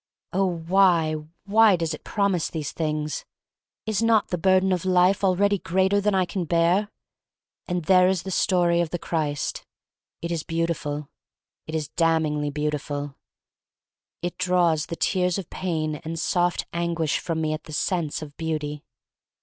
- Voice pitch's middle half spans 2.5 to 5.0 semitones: Yes, average, 3.1 semitones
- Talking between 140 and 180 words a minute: Yes, average, 160 wpm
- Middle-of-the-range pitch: Yes, medium, 170 Hz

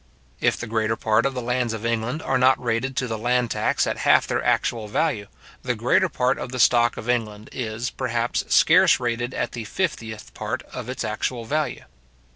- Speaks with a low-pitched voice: Yes, low, 120 Hz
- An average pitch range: No, narrow, 2.2 semitones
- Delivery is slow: No, average, 200 wpm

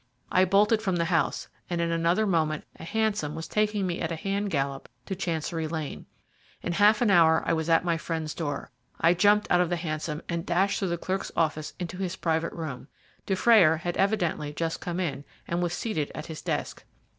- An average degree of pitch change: Yes, average, 3.1 semitones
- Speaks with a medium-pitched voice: Yes, medium, 170 Hz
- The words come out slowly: No, fast, 205 wpm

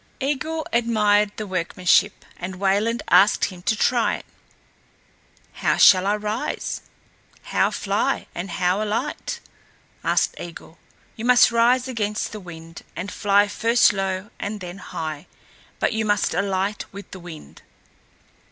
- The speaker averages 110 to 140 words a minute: Yes, slow, 135 wpm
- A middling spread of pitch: Yes, average, 3.4 semitones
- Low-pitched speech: No, high, 205 Hz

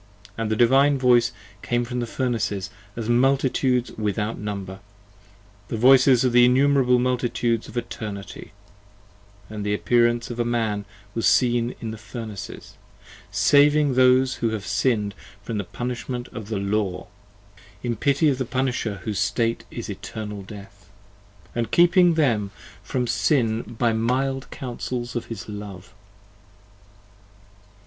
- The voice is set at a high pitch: No, low, 120 Hz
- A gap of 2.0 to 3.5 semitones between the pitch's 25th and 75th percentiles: Yes, average, 3.0 semitones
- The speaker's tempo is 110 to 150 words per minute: Yes, average, 140 wpm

